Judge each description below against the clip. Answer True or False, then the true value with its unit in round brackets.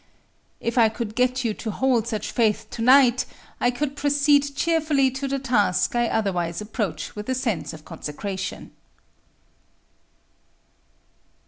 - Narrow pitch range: False (4.2 semitones)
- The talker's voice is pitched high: True (240 Hz)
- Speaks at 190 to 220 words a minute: False (135 wpm)